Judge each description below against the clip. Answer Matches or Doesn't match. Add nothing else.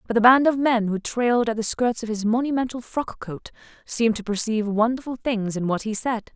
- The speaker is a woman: Matches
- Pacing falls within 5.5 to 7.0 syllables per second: Matches